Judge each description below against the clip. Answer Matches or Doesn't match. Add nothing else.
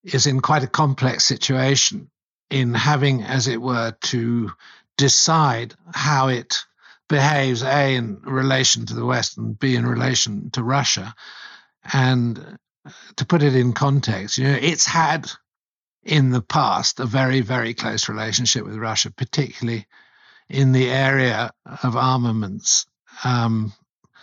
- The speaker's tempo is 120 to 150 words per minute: Matches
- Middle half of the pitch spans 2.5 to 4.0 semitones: Matches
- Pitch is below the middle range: Matches